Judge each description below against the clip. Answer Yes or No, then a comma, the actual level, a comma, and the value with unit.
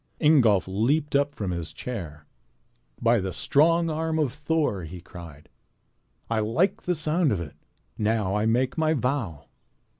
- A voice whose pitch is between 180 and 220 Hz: No, low, 120 Hz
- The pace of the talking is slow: No, average, 155 wpm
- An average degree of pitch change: No, wide, 8.3 semitones